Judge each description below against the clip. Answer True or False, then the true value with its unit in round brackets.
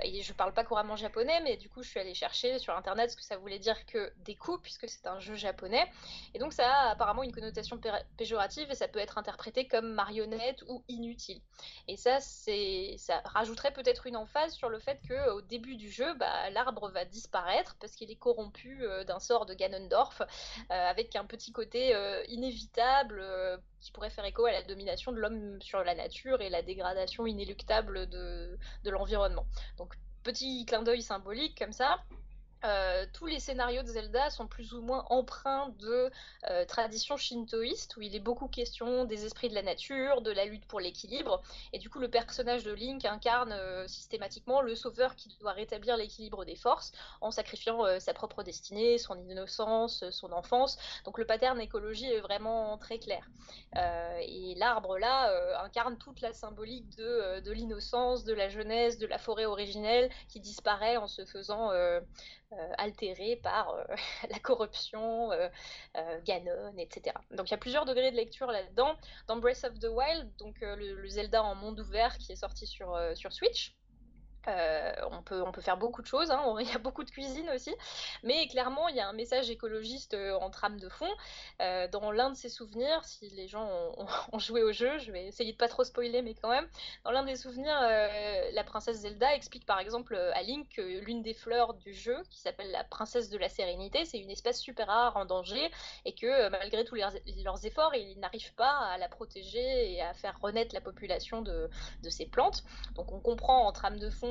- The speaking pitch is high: True (230 Hz)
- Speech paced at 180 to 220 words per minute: True (210 wpm)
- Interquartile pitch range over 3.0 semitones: True (3.7 semitones)